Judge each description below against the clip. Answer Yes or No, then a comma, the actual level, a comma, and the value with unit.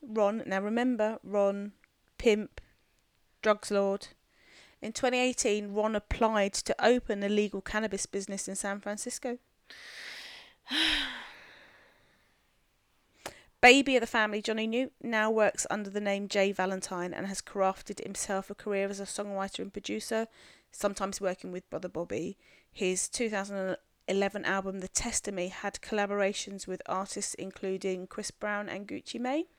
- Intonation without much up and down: Yes, narrow, 2.2 semitones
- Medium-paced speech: No, slow, 130 wpm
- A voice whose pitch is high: Yes, high, 205 Hz